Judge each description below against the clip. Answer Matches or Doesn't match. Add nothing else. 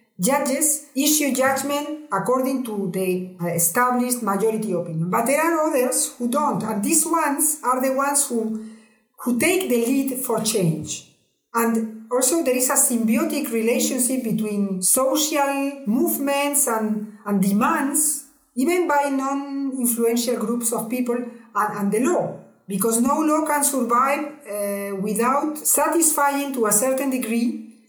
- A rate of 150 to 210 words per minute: Doesn't match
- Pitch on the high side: Matches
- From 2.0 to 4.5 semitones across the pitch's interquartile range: Matches